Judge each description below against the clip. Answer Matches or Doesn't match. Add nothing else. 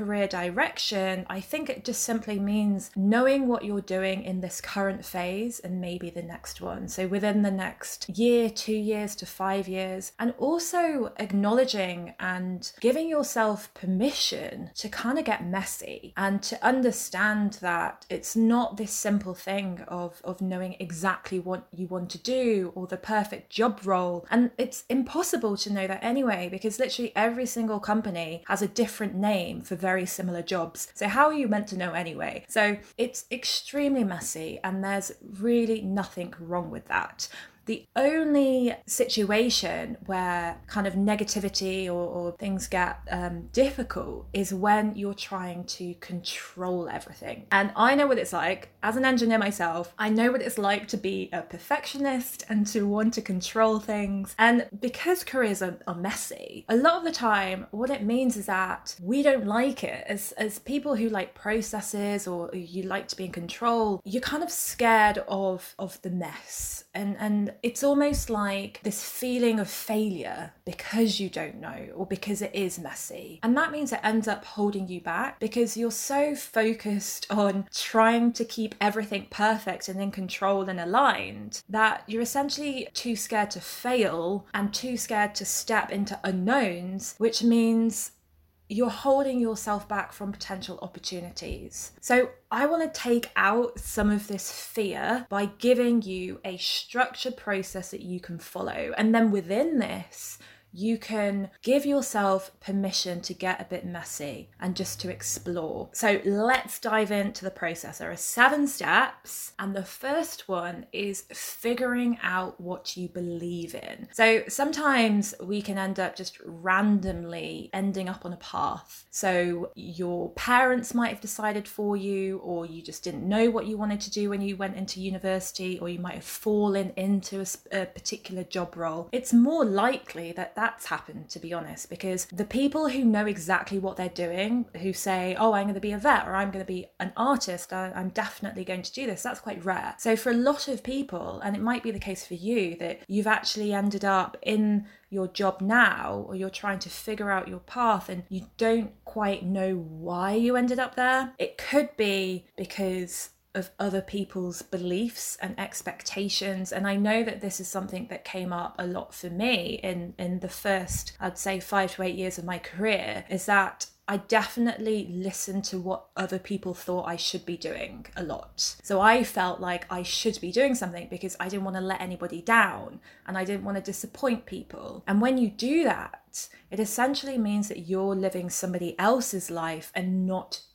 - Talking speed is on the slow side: Doesn't match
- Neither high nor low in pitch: Doesn't match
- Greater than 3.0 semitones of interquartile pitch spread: Matches